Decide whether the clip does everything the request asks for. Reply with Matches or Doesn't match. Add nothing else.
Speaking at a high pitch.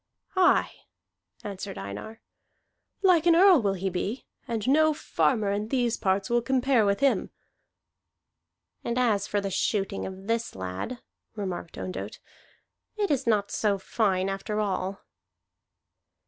Matches